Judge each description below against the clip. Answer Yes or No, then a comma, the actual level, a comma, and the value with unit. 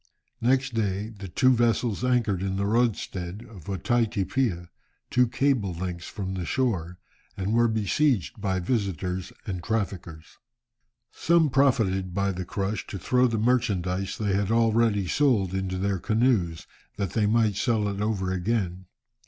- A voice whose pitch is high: No, low, 100 Hz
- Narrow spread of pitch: No, average, 3.8 semitones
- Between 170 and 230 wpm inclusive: No, average, 150 wpm